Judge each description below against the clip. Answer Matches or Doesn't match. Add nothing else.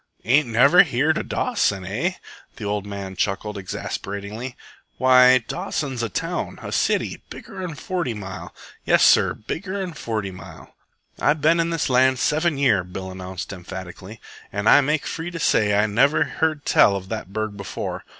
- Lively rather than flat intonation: Matches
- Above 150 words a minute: Matches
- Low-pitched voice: Matches